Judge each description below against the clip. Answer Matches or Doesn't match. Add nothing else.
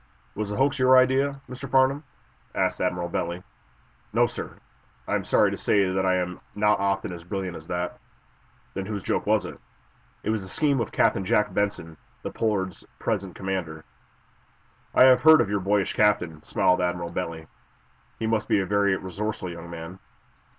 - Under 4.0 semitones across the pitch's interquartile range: Matches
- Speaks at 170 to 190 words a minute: Matches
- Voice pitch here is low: Matches